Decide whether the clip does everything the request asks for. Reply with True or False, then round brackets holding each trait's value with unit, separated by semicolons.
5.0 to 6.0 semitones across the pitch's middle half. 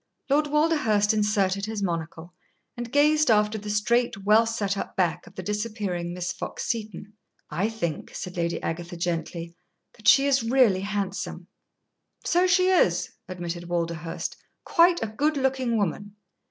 True (5.3 semitones)